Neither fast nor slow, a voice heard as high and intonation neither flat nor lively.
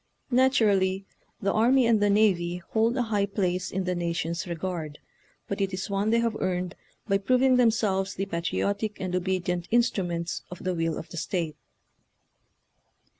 Yes: average, 165 wpm; high, 195 Hz; average, 3.6 semitones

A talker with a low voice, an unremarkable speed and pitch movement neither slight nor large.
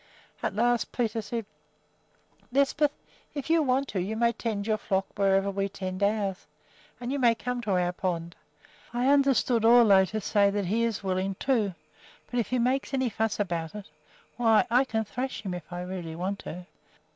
No: high, 215 Hz; average, 185 wpm; average, 4.1 semitones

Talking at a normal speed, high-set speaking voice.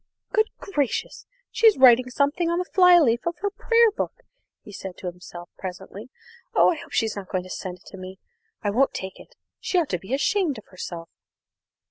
Yes: average, 190 wpm; very high, 250 Hz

